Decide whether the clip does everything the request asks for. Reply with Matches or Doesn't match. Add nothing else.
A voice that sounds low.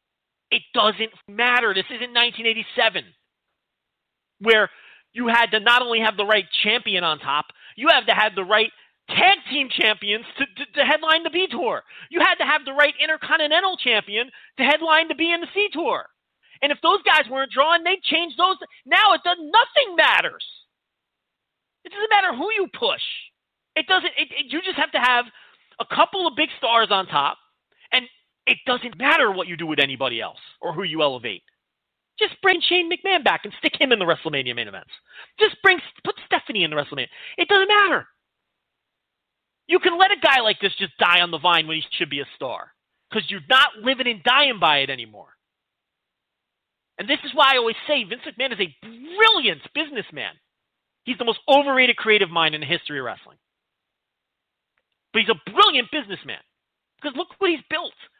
Doesn't match